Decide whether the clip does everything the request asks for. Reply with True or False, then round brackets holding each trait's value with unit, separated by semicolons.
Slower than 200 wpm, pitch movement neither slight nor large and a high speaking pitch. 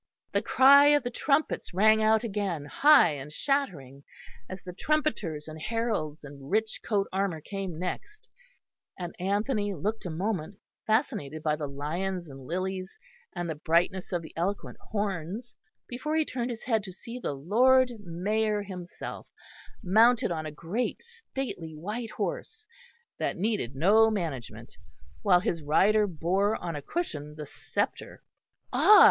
False (150 wpm; 5.9 semitones; 195 Hz)